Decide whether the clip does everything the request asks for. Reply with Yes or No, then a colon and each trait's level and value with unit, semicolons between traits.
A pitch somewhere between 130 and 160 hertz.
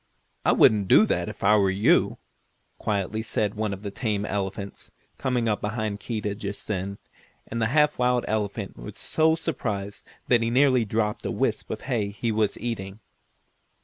No: low, 105 Hz